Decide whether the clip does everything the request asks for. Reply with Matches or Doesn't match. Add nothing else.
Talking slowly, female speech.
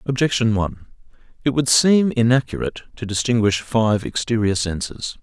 Doesn't match